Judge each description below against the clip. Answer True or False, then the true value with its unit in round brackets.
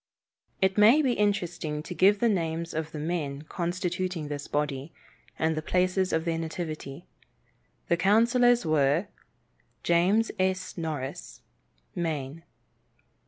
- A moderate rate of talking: False (120 wpm)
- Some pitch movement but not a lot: True (3.3 semitones)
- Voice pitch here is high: False (170 Hz)